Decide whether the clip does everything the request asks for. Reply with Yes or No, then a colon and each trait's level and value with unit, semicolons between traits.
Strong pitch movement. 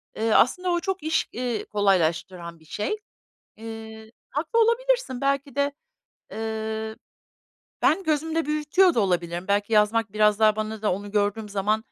Yes: wide, 6.2 semitones